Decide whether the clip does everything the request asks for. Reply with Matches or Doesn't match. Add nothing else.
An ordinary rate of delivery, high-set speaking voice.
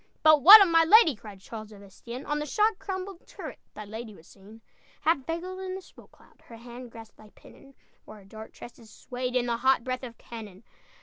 Doesn't match